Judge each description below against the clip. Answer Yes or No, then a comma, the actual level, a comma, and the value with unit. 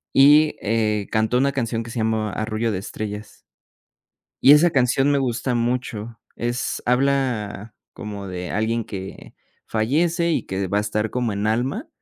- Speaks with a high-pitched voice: No, low, 115 Hz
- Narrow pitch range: No, average, 3.7 semitones